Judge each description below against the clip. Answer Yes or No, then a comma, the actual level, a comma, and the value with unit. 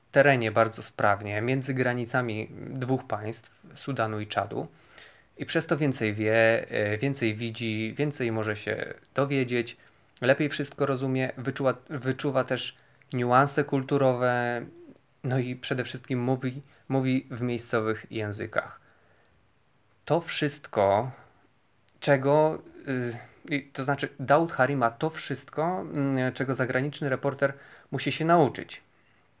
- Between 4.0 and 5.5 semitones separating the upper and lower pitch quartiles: No, average, 3.4 semitones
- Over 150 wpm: No, slow, 110 wpm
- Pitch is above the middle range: No, low, 130 Hz